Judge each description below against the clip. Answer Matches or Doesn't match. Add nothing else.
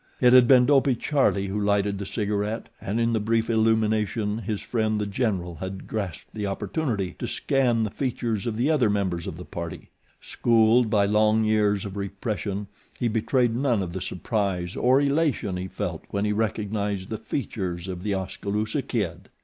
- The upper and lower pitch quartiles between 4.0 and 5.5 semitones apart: Doesn't match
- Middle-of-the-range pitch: Doesn't match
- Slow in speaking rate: Doesn't match